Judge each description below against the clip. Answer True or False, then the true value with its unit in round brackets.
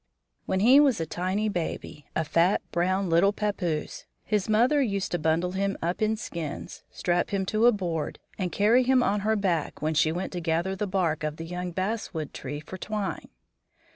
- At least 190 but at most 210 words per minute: True (195 wpm)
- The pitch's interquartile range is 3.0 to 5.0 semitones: True (4.0 semitones)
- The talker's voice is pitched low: False (185 Hz)